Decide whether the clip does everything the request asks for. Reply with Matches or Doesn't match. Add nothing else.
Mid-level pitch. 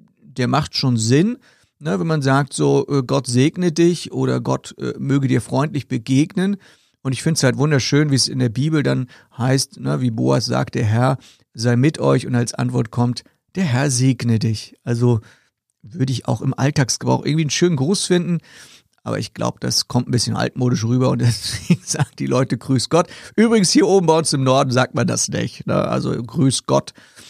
Doesn't match